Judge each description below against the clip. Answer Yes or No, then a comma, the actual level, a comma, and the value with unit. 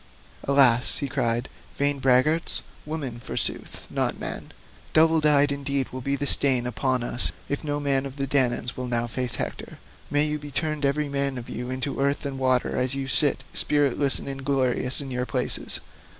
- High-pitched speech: No, low, 135 Hz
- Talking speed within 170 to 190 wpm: Yes, average, 180 wpm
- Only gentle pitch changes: Yes, narrow, 2.1 semitones